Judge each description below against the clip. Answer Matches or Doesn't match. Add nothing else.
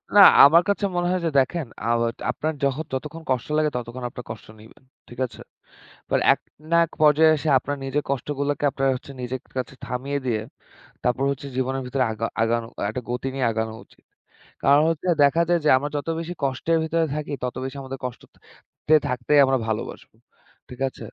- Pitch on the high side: Doesn't match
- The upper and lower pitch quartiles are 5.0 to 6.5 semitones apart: Doesn't match